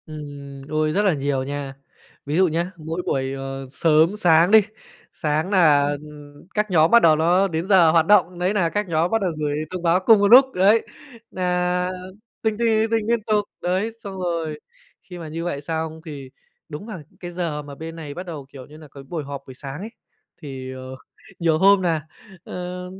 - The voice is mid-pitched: Yes, medium, 165 Hz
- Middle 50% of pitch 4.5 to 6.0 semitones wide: No, average, 3.9 semitones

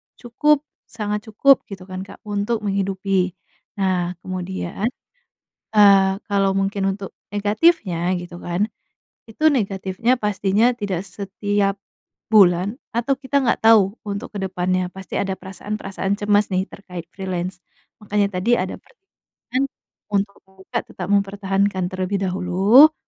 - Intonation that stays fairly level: Yes, narrow, 2.0 semitones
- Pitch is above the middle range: Yes, high, 195 Hz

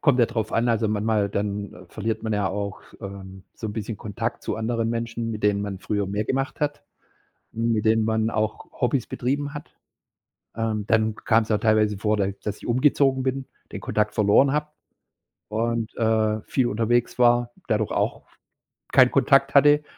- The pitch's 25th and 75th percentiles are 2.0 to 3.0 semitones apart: Yes, narrow, 2.4 semitones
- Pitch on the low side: Yes, low, 110 Hz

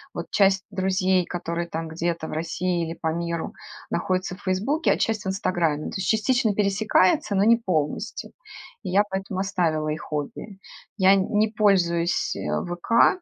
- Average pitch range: Yes, average, 3.0 semitones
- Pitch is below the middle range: No, medium, 185 Hz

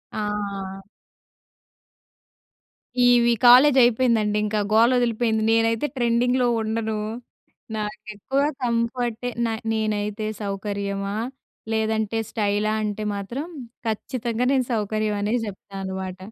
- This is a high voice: Yes, high, 220 Hz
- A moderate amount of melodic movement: No, narrow, 2.3 semitones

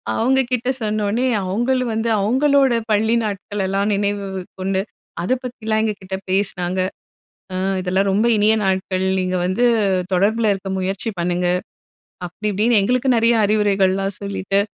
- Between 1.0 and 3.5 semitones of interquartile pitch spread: Yes, average, 2.9 semitones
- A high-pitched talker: Yes, high, 205 Hz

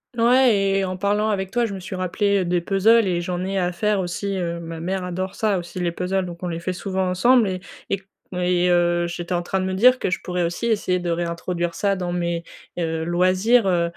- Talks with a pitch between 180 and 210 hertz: Yes, medium, 185 Hz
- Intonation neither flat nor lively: No, narrow, 2.2 semitones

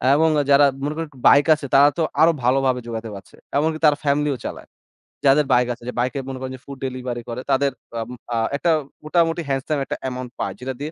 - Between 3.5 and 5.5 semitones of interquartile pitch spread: No, average, 2.7 semitones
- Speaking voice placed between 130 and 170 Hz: Yes, low, 135 Hz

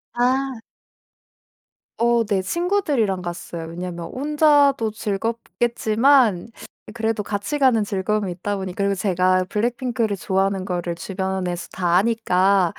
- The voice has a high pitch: Yes, high, 205 Hz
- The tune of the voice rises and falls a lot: No, average, 4.3 semitones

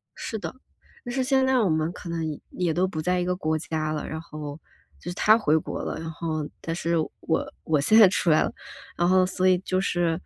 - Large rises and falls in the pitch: No, average, 2.8 semitones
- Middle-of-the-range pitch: Yes, medium, 170 Hz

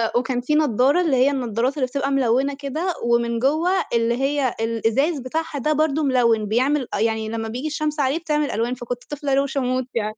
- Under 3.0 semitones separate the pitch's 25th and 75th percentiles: No, average, 3.8 semitones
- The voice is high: Yes, very high, 265 Hz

